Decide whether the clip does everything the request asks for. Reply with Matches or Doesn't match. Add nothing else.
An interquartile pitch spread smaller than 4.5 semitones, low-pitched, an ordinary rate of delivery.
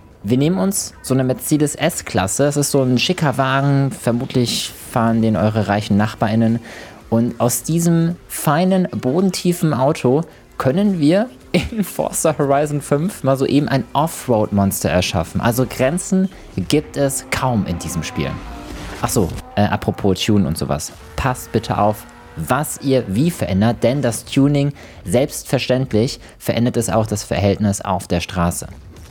Doesn't match